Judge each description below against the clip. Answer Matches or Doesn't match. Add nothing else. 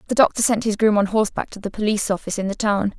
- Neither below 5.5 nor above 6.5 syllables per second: Doesn't match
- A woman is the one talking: Matches